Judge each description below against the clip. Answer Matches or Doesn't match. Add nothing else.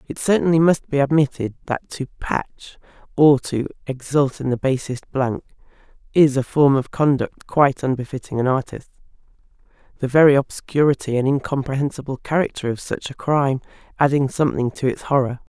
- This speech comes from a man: Doesn't match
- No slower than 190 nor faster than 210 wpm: Doesn't match